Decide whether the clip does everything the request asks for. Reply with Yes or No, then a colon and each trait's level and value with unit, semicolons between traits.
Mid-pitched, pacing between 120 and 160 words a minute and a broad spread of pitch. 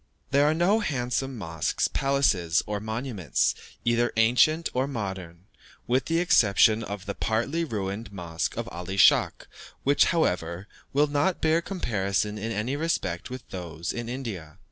No: low, 115 Hz; average, 145 wpm; wide, 6.5 semitones